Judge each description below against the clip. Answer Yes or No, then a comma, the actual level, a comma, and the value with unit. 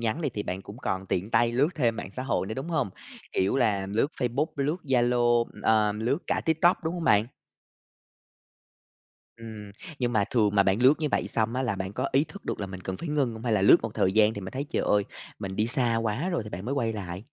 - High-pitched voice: No, low, 115 Hz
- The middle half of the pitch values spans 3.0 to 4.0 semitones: No, average, 4.5 semitones